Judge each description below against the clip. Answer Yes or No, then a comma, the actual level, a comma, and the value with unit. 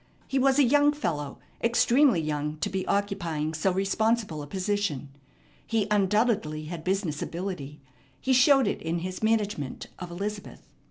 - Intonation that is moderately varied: No, wide, 6.0 semitones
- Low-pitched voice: No, high, 195 Hz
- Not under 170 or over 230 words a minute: No, average, 150 wpm